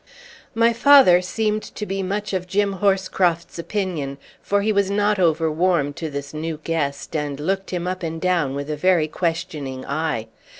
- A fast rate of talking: No, average, 175 wpm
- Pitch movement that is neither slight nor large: Yes, average, 4.1 semitones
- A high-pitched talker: No, medium, 175 Hz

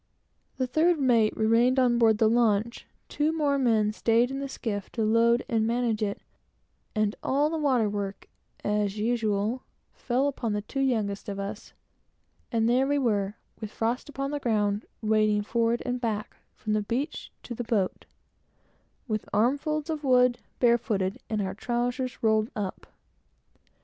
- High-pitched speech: Yes, high, 230 Hz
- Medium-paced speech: Yes, average, 160 wpm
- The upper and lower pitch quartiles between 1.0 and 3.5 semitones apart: Yes, average, 3.0 semitones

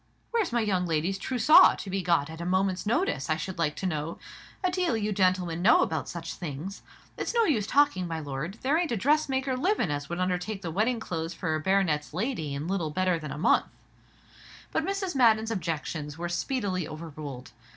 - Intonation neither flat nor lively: No, wide, 6.2 semitones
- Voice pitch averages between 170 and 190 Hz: Yes, medium, 185 Hz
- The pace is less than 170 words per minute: No, average, 195 wpm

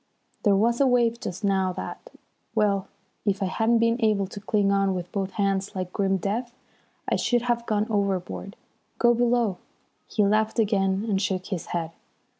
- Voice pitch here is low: No, high, 200 Hz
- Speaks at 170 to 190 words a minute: Yes, average, 175 wpm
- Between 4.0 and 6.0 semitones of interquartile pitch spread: No, average, 2.9 semitones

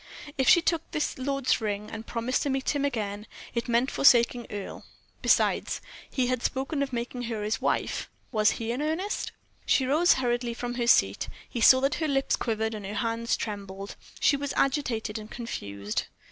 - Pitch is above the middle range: Yes, high, 240 Hz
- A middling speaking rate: Yes, average, 185 wpm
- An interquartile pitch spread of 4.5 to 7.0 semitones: No, average, 3.7 semitones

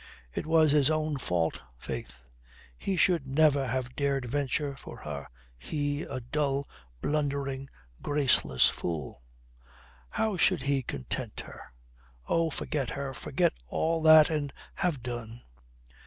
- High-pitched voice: No, medium, 140 Hz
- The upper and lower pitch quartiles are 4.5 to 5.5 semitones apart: No, average, 3.6 semitones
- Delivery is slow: Yes, slow, 125 wpm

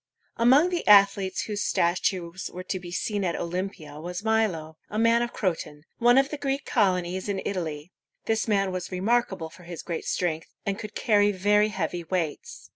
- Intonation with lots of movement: No, average, 3.8 semitones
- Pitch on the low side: No, high, 190 Hz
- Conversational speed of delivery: Yes, average, 180 wpm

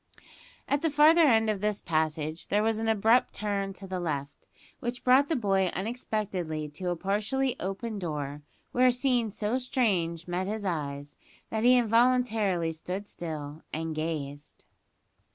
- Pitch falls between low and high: No, high, 200 Hz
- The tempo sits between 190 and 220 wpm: No, average, 155 wpm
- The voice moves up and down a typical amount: No, wide, 6.4 semitones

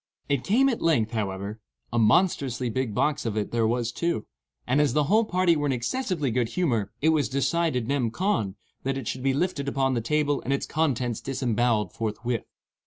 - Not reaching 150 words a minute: No, average, 185 wpm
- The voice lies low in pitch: Yes, low, 130 Hz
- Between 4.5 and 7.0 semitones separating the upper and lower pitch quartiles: Yes, average, 4.9 semitones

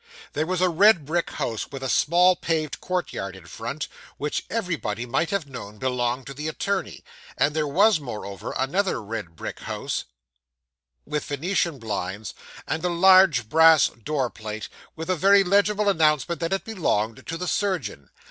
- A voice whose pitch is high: No, medium, 155 Hz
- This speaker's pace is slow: No, average, 165 wpm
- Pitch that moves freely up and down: Yes, wide, 7.1 semitones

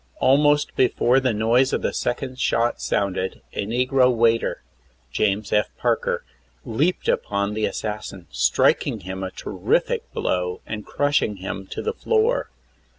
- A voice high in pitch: No, low, 115 Hz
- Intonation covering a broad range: No, average, 4.5 semitones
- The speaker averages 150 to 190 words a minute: No, average, 140 wpm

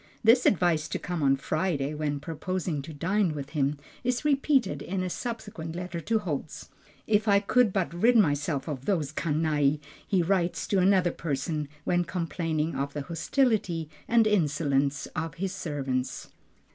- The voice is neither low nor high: Yes, medium, 165 Hz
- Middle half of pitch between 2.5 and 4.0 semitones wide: No, average, 4.8 semitones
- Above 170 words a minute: No, average, 160 wpm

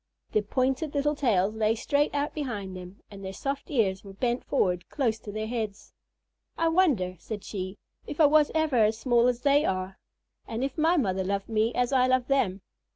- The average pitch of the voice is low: No, high, 230 Hz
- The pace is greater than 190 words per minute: Yes, average, 200 wpm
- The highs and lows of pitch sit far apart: Yes, wide, 5.9 semitones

